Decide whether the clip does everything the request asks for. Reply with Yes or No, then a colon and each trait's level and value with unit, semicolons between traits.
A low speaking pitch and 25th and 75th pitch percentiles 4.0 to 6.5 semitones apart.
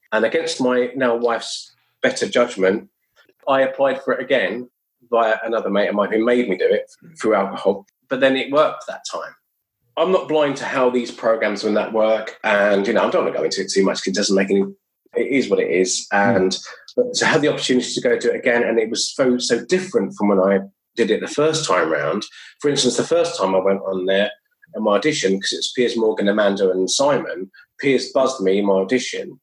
Yes: low, 120 Hz; wide, 5.4 semitones